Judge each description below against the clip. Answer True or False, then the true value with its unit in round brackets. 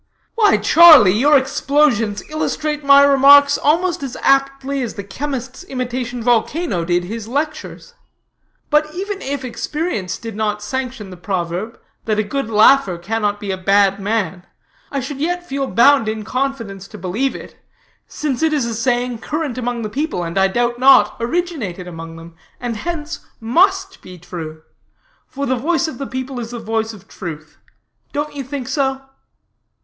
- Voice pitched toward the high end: True (245 Hz)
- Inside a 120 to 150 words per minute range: False (165 wpm)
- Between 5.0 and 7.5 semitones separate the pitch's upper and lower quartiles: True (5.4 semitones)